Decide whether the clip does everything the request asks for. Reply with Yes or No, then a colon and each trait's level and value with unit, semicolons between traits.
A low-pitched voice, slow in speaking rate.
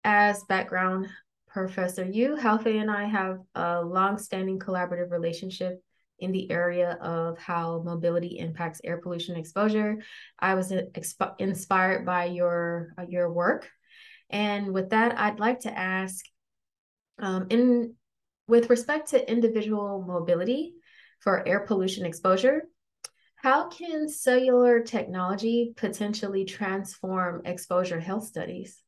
No: high, 190 Hz; slow, 115 wpm